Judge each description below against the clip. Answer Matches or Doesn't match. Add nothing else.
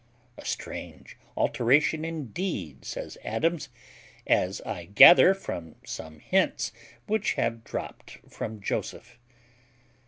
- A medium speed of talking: Doesn't match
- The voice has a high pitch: Doesn't match